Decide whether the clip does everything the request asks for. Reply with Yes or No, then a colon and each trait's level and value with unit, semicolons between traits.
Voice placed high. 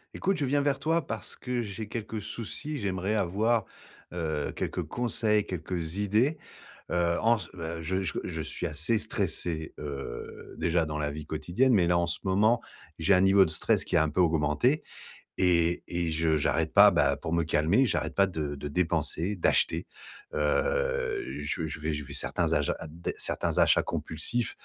No: very low, 90 Hz